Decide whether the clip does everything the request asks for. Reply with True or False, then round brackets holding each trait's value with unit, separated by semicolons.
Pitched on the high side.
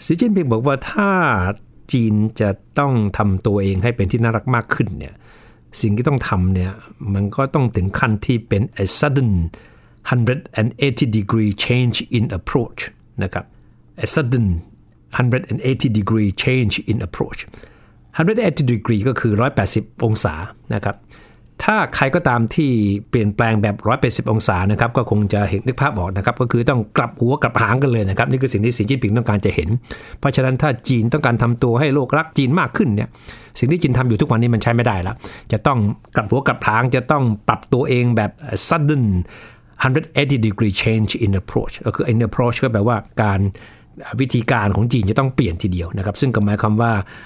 False (115 Hz)